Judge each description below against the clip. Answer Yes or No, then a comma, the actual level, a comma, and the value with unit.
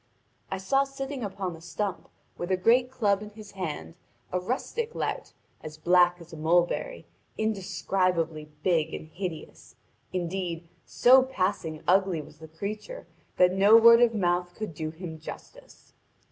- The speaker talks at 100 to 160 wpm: Yes, average, 150 wpm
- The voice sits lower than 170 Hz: No, medium, 185 Hz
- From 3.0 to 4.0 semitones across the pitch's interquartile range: No, average, 4.5 semitones